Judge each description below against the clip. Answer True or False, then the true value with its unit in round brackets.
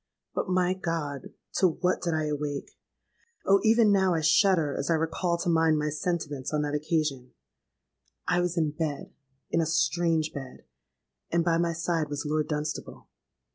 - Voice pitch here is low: False (160 Hz)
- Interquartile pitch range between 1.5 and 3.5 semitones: True (2.6 semitones)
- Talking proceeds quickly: False (165 wpm)